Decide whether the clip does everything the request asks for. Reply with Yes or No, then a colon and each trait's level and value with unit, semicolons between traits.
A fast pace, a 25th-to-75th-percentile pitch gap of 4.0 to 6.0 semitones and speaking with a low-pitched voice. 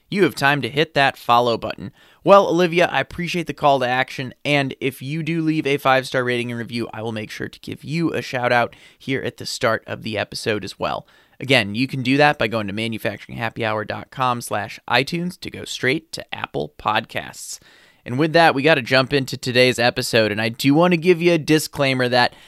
Yes: fast, 210 wpm; average, 4.6 semitones; low, 130 Hz